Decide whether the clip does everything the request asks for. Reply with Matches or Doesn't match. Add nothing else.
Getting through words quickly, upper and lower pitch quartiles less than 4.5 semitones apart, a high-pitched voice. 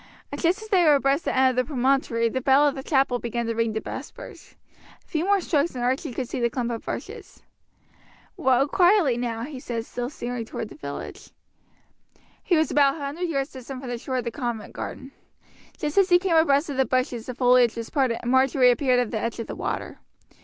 Matches